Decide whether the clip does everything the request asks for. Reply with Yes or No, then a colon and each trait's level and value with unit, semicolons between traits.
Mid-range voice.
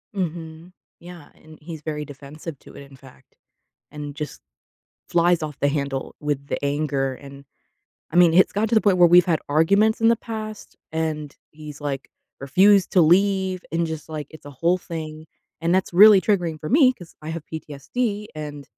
Yes: medium, 160 Hz